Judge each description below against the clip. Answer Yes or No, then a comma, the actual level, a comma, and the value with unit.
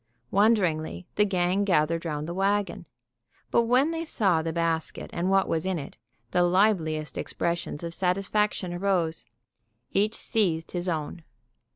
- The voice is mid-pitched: Yes, medium, 180 Hz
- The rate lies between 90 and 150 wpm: Yes, average, 145 wpm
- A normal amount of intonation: Yes, average, 3.4 semitones